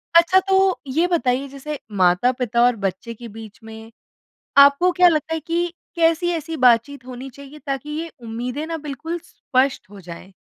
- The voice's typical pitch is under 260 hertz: No, very high, 275 Hz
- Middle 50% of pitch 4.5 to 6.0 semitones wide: Yes, wide, 5.4 semitones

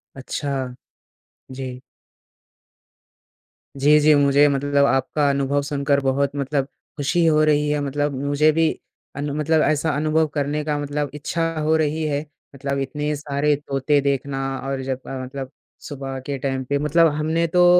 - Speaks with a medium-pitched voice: Yes, medium, 145 Hz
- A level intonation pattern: Yes, narrow, 1.7 semitones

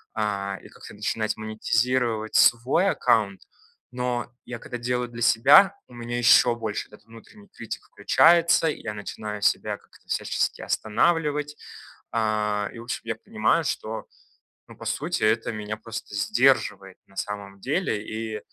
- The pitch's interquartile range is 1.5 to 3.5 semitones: Yes, average, 2.8 semitones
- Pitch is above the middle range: No, low, 115 Hz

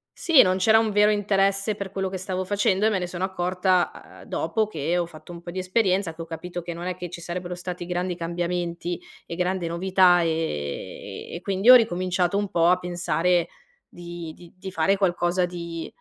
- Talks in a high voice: No, medium, 180 Hz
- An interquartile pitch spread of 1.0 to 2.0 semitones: Yes, narrow, 1.7 semitones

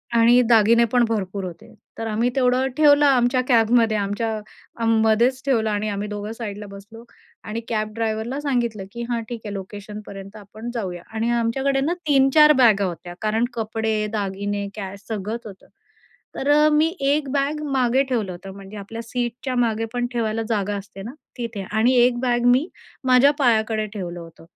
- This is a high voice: Yes, high, 225 Hz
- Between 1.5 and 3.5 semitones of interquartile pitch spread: Yes, average, 3.1 semitones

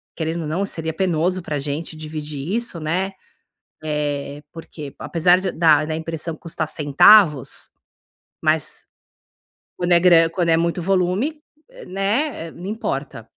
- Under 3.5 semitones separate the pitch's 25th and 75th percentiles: Yes, average, 3.0 semitones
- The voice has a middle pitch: Yes, medium, 165 Hz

